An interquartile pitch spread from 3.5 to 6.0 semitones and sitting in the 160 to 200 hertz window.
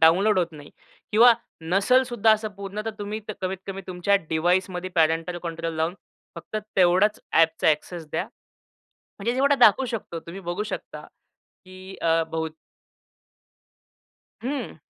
Yes: average, 4.2 semitones; medium, 185 Hz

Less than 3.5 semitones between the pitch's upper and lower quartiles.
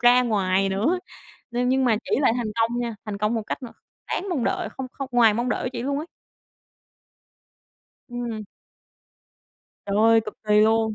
Yes: narrow, 2.5 semitones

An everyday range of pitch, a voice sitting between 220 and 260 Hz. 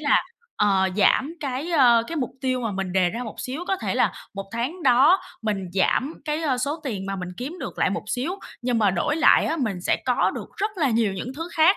No: wide, 7.2 semitones; very high, 250 Hz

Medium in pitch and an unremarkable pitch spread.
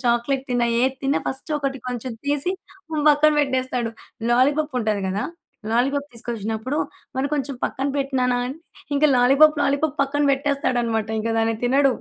No: very high, 265 Hz; average, 3.0 semitones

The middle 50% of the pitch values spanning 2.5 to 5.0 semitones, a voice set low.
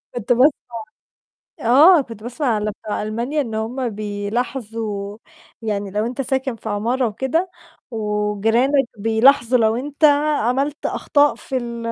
No: average, 3.7 semitones; high, 235 Hz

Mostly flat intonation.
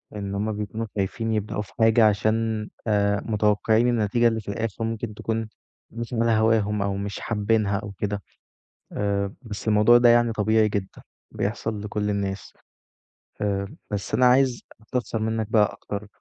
Yes: narrow, 1.7 semitones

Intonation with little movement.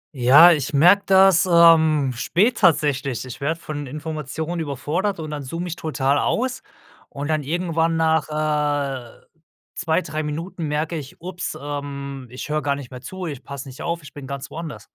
No: average, 3.1 semitones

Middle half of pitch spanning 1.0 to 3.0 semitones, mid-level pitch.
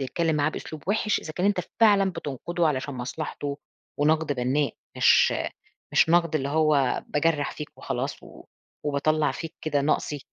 Yes: narrow, 2.4 semitones; medium, 150 Hz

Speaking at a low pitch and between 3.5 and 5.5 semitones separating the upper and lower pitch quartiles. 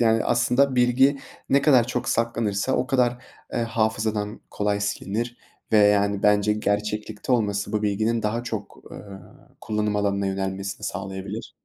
No: low, 105 Hz; average, 2.7 semitones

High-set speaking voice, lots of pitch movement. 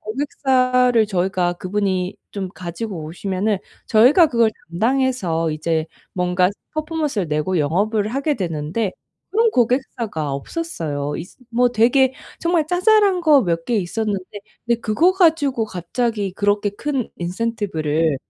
Yes: high, 215 Hz; wide, 6.6 semitones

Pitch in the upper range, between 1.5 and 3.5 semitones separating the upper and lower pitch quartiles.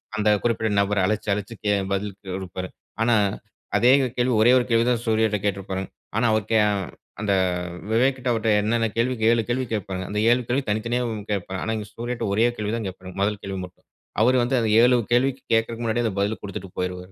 No: low, 110 Hz; average, 2.9 semitones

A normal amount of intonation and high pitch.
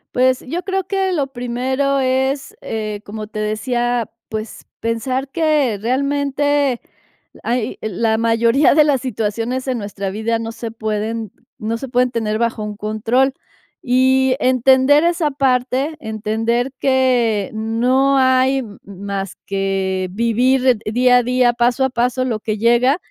Yes: average, 3.2 semitones; high, 245 Hz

